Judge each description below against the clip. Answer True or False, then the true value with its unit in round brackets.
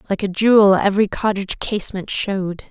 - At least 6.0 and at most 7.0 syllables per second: True (6.1 syllables/s)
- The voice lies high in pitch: True (200 Hz)